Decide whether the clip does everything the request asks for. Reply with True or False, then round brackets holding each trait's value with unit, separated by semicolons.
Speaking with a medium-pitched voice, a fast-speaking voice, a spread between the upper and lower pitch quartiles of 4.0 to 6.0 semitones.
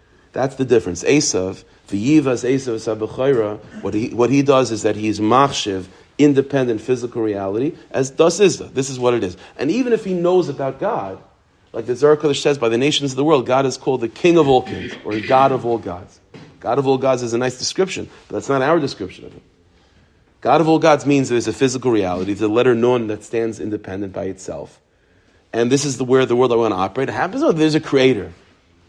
False (125 Hz; 220 wpm; 4.7 semitones)